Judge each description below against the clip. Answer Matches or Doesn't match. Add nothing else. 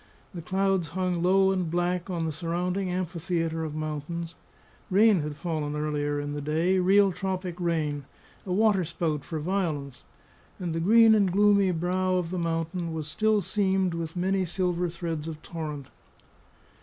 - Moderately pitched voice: Matches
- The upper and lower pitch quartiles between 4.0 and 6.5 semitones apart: Doesn't match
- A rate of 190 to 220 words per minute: Doesn't match